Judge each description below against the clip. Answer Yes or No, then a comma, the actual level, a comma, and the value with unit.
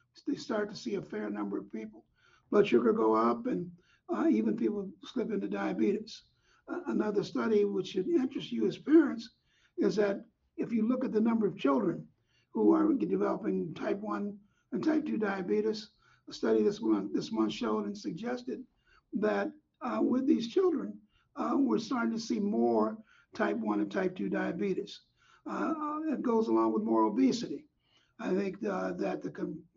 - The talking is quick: No, average, 175 wpm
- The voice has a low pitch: No, high, 210 Hz